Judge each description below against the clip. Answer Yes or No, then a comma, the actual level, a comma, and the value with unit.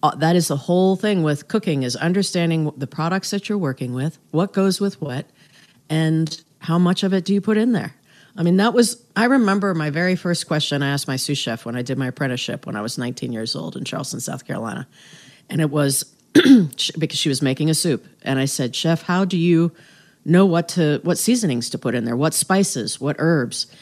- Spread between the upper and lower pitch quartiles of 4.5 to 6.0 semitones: Yes, average, 4.8 semitones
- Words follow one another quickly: Yes, fast, 225 wpm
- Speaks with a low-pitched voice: No, medium, 160 Hz